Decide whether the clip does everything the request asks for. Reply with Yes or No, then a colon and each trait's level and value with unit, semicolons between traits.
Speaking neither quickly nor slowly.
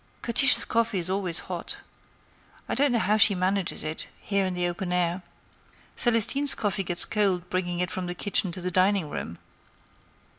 Yes: average, 175 wpm